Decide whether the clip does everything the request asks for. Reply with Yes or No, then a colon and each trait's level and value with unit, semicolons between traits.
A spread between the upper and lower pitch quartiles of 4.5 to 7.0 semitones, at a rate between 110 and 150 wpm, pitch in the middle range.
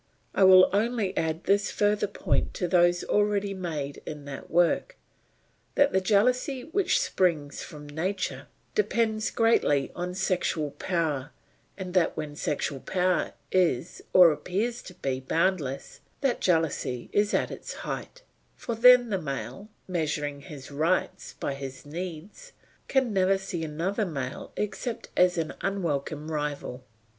Yes: wide, 5.5 semitones; average, 140 wpm; medium, 180 Hz